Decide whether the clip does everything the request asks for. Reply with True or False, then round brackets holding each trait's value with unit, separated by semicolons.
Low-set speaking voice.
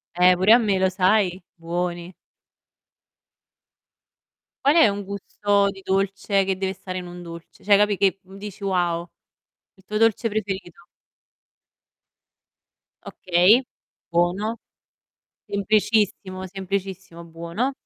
False (190 Hz)